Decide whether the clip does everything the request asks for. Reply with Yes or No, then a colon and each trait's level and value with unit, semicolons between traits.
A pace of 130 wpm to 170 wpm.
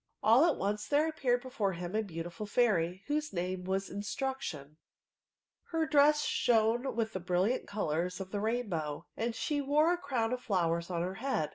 No: average, 180 wpm